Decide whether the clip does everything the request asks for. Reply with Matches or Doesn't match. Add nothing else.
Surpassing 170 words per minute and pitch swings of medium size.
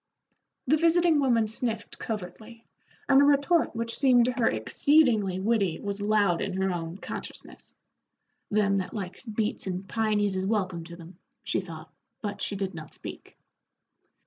Doesn't match